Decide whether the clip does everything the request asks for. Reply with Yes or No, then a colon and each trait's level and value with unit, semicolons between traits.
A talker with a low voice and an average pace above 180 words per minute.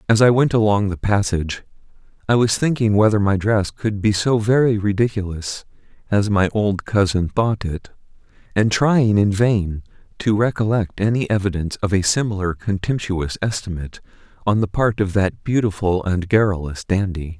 No: low, 100 Hz; average, 155 wpm